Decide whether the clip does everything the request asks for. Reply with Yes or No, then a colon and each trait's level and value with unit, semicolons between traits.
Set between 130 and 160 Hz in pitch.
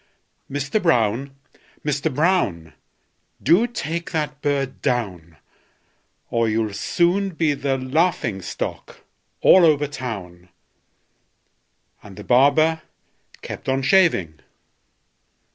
Yes: medium, 140 Hz